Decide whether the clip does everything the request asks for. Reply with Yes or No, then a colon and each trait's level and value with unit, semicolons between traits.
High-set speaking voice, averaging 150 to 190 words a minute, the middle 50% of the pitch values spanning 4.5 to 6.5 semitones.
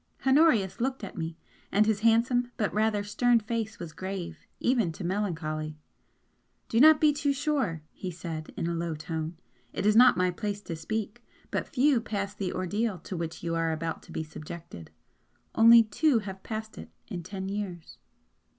Yes: high, 200 Hz; average, 180 wpm; average, 5.3 semitones